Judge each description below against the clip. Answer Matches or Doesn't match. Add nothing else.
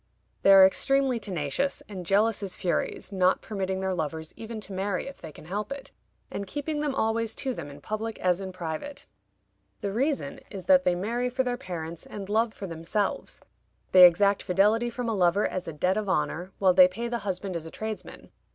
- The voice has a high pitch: Matches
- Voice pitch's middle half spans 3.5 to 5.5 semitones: Matches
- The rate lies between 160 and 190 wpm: Doesn't match